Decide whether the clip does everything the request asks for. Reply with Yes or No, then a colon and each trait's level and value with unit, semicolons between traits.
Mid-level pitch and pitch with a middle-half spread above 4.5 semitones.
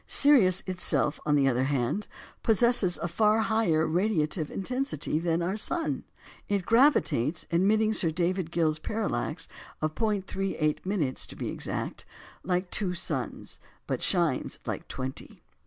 Yes: medium, 180 Hz; average, 5.3 semitones